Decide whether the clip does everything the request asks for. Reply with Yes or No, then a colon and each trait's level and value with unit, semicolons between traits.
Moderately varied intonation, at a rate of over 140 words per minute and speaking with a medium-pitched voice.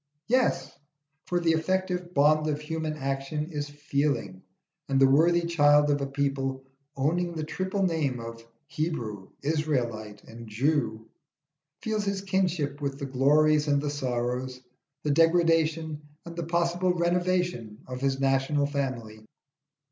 No: average, 3.9 semitones; slow, 135 wpm; medium, 150 Hz